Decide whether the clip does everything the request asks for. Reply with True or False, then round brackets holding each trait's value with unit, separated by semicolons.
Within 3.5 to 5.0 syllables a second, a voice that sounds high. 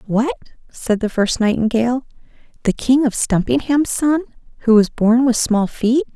True (4.8 syllables/s; 240 Hz)